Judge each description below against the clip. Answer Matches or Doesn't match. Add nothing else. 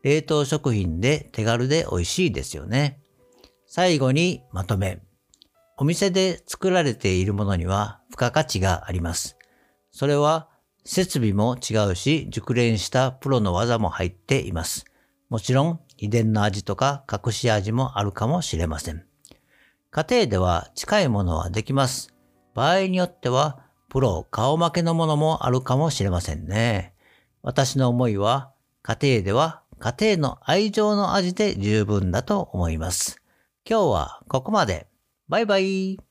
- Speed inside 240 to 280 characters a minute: Matches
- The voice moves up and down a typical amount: Doesn't match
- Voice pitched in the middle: Doesn't match